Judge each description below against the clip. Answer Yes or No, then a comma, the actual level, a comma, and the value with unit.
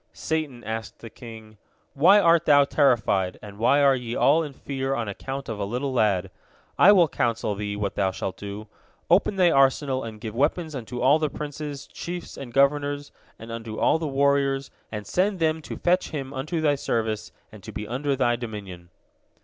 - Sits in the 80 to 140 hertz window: Yes, low, 135 Hz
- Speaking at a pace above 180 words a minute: Yes, average, 190 wpm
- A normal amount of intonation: Yes, average, 4.9 semitones